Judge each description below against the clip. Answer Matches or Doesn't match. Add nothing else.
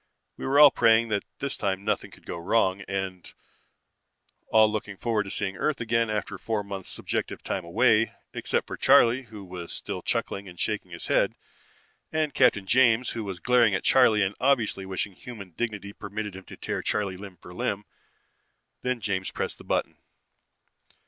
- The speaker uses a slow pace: Doesn't match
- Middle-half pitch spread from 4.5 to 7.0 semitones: Doesn't match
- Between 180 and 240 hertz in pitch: Doesn't match